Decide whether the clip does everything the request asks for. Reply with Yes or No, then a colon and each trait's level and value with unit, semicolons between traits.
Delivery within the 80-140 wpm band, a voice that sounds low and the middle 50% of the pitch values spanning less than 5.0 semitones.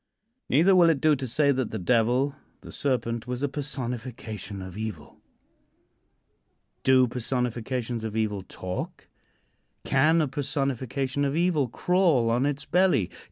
Yes: slow, 135 wpm; low, 130 Hz; average, 3.8 semitones